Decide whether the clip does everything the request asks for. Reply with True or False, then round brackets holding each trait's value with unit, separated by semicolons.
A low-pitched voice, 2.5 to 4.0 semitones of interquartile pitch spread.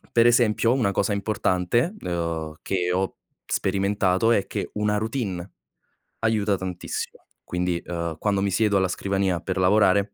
True (100 Hz; 2.8 semitones)